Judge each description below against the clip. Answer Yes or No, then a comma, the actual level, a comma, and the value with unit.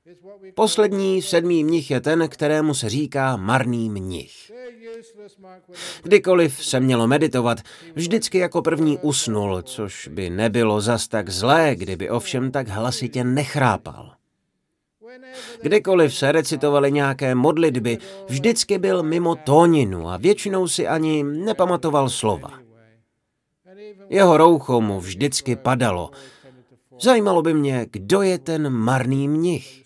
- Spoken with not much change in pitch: No, wide, 6.2 semitones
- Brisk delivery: No, slow, 115 wpm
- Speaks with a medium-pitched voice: Yes, medium, 145 Hz